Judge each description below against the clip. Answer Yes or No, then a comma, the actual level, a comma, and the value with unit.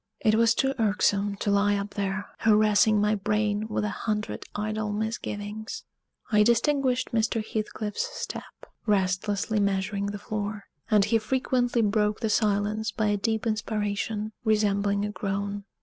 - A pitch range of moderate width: No, narrow, 1.2 semitones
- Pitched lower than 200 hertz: No, high, 210 Hz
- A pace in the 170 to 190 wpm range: No, average, 145 wpm